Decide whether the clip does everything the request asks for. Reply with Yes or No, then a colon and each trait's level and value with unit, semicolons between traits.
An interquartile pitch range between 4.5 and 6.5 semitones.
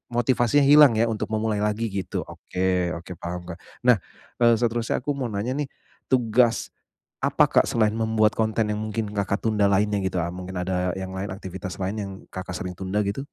No: average, 3.3 semitones